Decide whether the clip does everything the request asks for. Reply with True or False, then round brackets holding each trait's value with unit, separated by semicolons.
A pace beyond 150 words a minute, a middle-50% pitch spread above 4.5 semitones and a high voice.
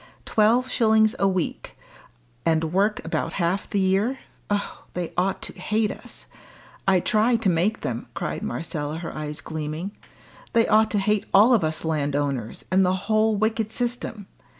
True (160 wpm; 5.0 semitones; 195 Hz)